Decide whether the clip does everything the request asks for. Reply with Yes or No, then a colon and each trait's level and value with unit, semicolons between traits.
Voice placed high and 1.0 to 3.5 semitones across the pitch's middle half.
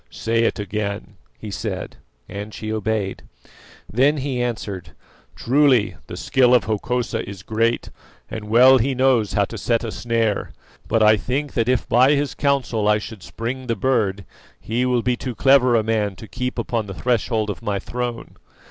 No: low, 115 Hz; average, 3.0 semitones